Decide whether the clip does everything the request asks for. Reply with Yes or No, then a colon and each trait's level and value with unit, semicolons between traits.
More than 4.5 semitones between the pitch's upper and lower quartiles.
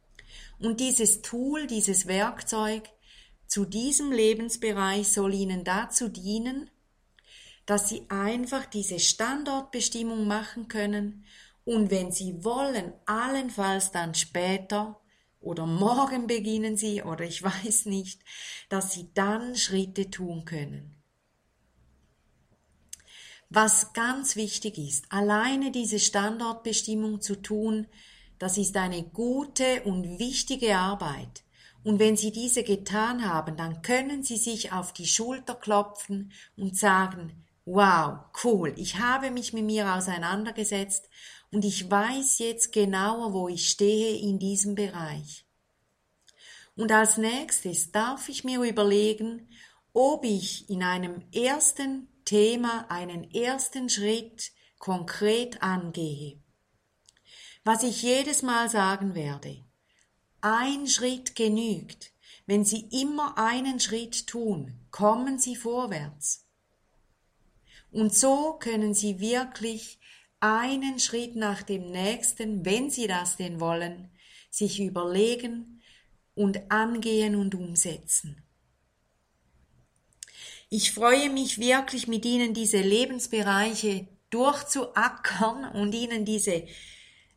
No: average, 3.7 semitones